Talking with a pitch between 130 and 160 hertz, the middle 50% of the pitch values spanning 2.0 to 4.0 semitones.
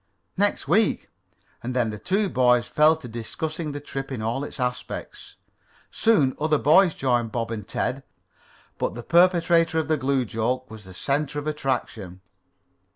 No: low, 135 Hz; average, 4.9 semitones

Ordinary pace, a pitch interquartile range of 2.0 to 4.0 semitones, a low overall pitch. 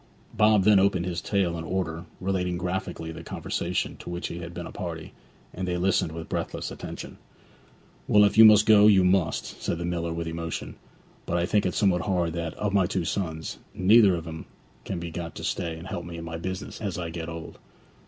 No: fast, 220 wpm; narrow, 2.4 semitones; very low, 90 Hz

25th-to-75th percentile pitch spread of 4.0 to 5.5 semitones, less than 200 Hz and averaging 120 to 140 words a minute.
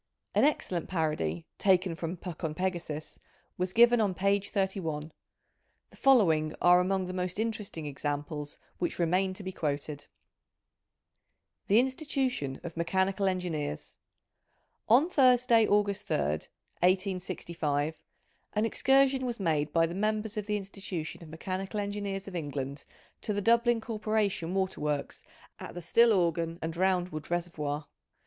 Yes: average, 4.5 semitones; medium, 185 Hz; slow, 135 wpm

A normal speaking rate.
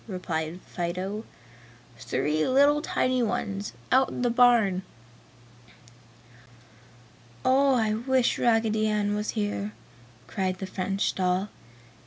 No: slow, 105 wpm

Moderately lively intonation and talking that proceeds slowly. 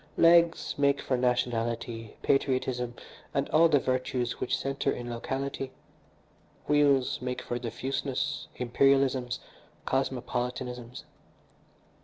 No: narrow, 1.9 semitones; slow, 95 wpm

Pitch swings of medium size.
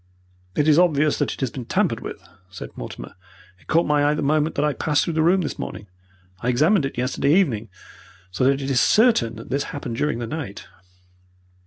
Yes: average, 3.9 semitones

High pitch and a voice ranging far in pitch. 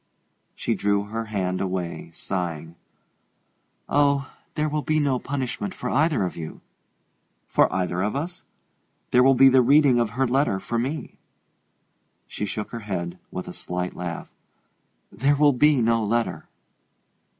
No: low, 115 Hz; wide, 7.1 semitones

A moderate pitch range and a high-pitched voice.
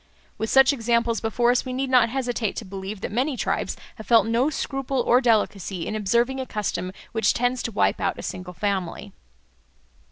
Yes: average, 3.4 semitones; high, 235 Hz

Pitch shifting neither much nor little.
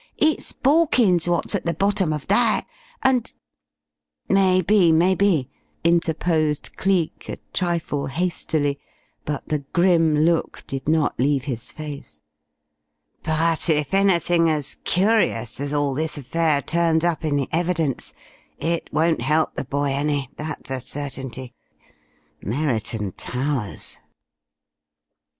Yes: average, 3.6 semitones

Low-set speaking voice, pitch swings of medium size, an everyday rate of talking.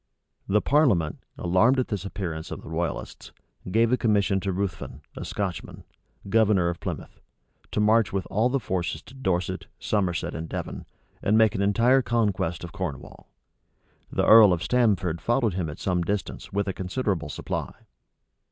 Yes: low, 100 Hz; average, 4.0 semitones; average, 160 wpm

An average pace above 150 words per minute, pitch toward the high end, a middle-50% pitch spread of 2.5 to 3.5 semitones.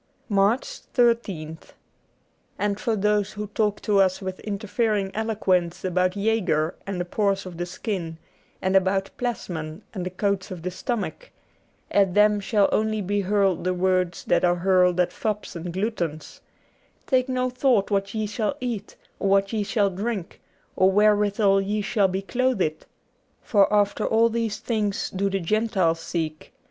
Yes: average, 170 wpm; high, 200 Hz; average, 2.8 semitones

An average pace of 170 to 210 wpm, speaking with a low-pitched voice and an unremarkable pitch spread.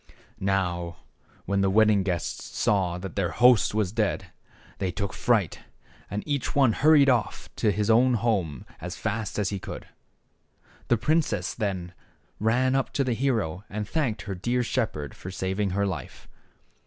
No: average, 160 wpm; low, 105 Hz; average, 4.2 semitones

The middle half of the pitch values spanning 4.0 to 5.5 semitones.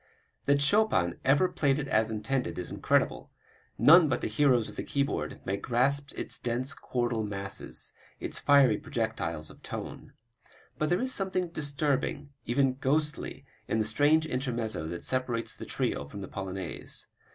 Yes: average, 4.9 semitones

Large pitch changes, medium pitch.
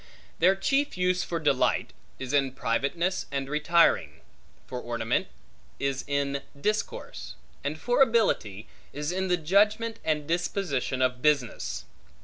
Yes: wide, 5.7 semitones; medium, 150 Hz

